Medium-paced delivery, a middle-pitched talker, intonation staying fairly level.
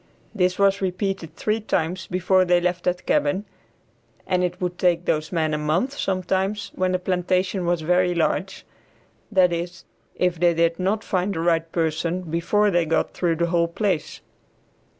Yes: average, 170 wpm; medium, 180 Hz; narrow, 1.8 semitones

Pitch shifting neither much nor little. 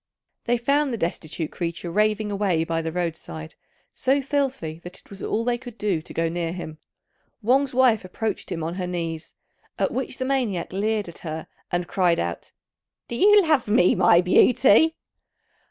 No: wide, 6.6 semitones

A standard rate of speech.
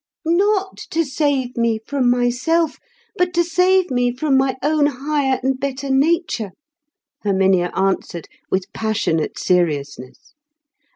No: slow, 120 wpm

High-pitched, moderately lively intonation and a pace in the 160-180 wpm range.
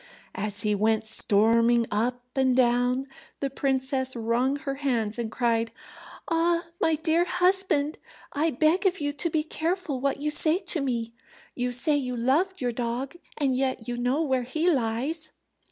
Yes: very high, 265 Hz; average, 4.6 semitones; average, 165 wpm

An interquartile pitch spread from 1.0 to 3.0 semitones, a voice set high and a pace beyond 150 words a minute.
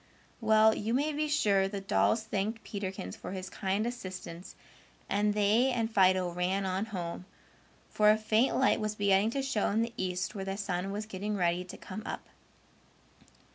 Yes: average, 2.7 semitones; high, 205 Hz; average, 175 wpm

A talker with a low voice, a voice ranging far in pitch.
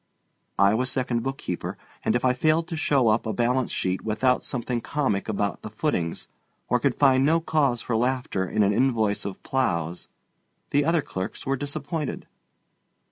No: low, 125 Hz; average, 4.4 semitones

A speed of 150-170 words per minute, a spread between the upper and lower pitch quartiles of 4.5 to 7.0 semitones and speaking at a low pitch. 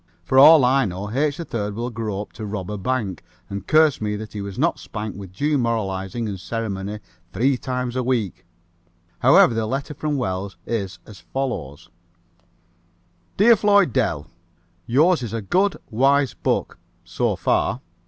Yes: average, 165 wpm; average, 5.3 semitones; low, 115 Hz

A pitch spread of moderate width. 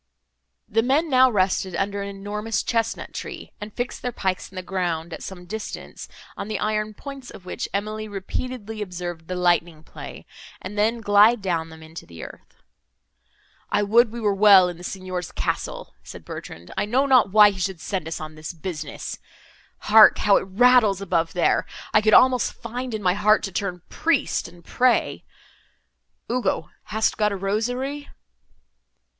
Yes: average, 3.7 semitones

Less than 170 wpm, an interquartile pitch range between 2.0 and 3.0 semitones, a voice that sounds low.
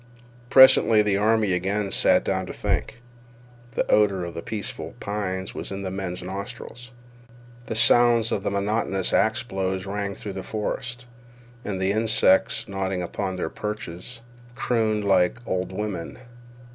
Yes: average, 145 wpm; average, 2.7 semitones; low, 100 Hz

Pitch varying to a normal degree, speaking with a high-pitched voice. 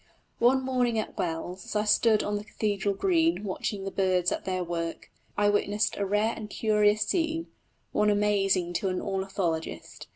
No: narrow, 2.2 semitones; high, 205 Hz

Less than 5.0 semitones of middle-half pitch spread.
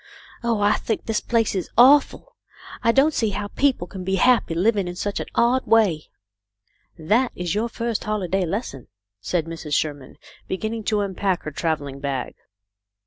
No: wide, 5.4 semitones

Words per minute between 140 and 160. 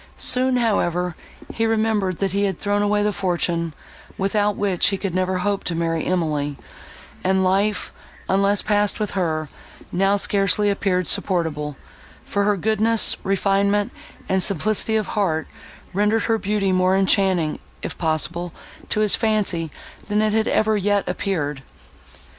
Yes: average, 145 wpm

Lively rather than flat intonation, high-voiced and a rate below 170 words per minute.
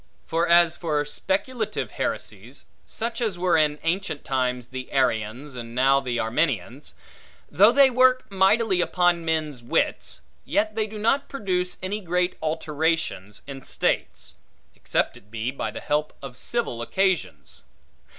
No: wide, 6.7 semitones; medium, 160 Hz; average, 140 wpm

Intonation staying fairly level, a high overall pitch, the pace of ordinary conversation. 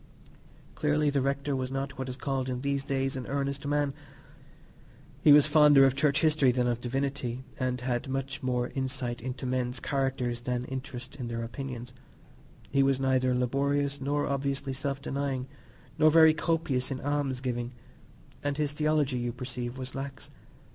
No: narrow, 1.9 semitones; low, 135 Hz; average, 165 wpm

